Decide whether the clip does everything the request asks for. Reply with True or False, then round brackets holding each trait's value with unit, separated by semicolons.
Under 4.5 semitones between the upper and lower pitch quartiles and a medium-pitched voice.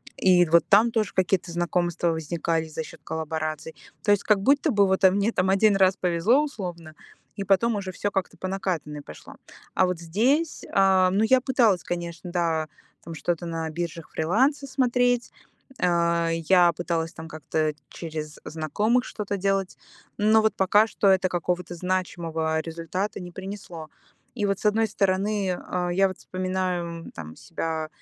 True (3.3 semitones; 180 Hz)